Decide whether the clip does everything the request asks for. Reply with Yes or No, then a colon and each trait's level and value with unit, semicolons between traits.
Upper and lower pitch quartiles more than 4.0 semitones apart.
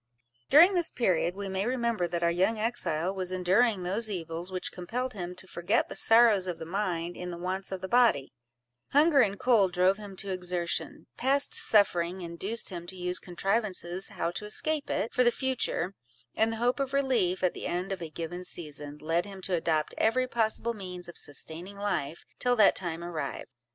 Yes: average, 4.5 semitones